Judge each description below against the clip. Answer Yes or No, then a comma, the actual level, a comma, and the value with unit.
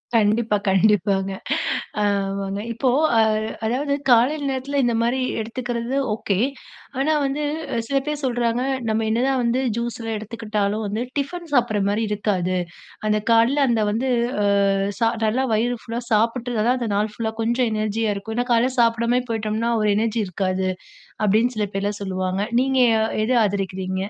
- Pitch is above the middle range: Yes, high, 225 Hz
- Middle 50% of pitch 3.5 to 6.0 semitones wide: No, average, 2.9 semitones